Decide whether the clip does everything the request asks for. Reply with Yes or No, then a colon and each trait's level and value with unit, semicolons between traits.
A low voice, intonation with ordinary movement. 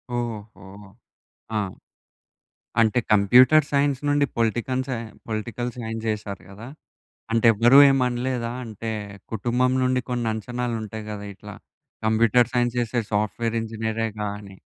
No: low, 115 Hz; narrow, 2.3 semitones